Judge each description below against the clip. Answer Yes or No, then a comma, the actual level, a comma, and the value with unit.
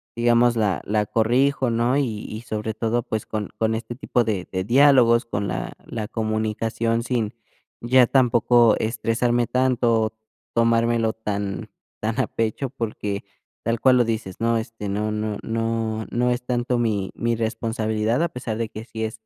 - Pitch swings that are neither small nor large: No, narrow, 1.7 semitones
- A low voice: Yes, low, 115 Hz